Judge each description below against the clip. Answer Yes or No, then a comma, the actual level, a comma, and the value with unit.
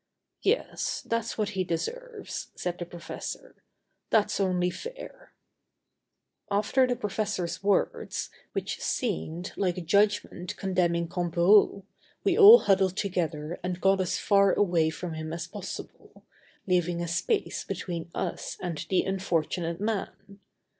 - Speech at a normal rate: No, slow, 125 wpm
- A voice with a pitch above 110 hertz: Yes, medium, 185 Hz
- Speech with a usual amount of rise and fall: Yes, average, 3.1 semitones